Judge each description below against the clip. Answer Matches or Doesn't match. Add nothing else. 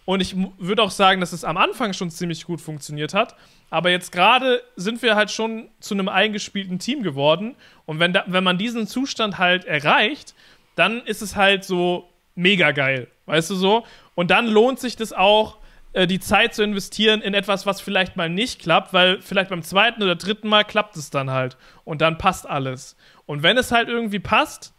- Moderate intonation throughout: Matches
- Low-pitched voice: Doesn't match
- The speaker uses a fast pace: Matches